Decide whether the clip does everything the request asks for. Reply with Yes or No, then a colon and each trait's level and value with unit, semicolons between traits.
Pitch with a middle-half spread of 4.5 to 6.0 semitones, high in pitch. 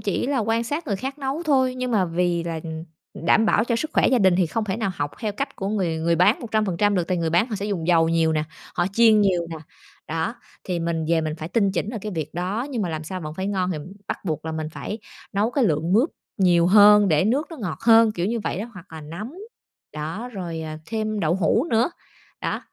Yes: average, 5.2 semitones; high, 195 Hz